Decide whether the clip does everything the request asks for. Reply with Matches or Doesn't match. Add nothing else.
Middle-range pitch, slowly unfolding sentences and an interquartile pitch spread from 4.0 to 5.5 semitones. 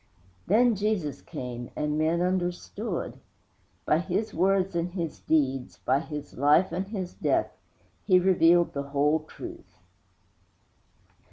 Matches